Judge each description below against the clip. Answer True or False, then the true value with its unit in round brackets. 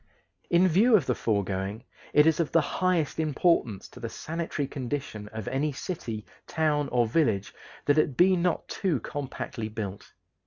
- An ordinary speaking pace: True (160 wpm)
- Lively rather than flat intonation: True (6.8 semitones)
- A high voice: False (145 Hz)